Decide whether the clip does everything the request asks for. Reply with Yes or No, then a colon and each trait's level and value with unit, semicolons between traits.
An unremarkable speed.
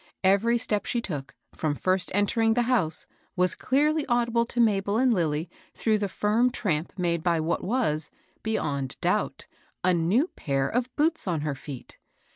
Yes: average, 165 wpm